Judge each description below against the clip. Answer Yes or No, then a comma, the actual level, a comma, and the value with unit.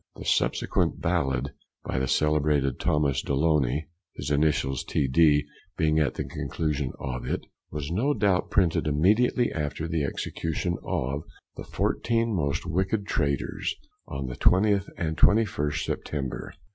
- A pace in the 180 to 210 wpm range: No, slow, 135 wpm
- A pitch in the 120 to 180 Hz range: No, very low, 75 Hz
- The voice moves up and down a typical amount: Yes, average, 4.2 semitones